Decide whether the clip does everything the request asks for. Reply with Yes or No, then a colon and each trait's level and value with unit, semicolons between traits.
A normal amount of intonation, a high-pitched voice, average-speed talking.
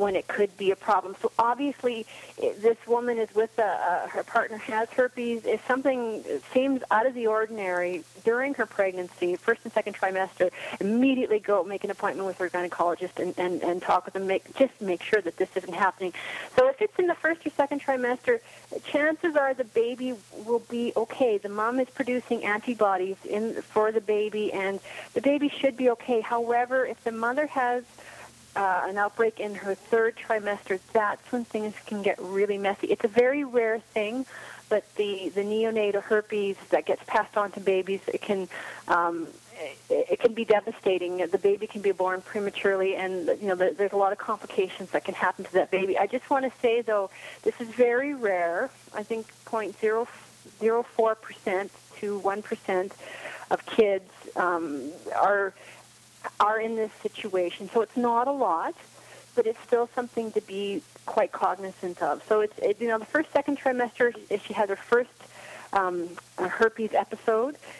Yes: average, 3.9 semitones; high, 220 Hz; average, 180 wpm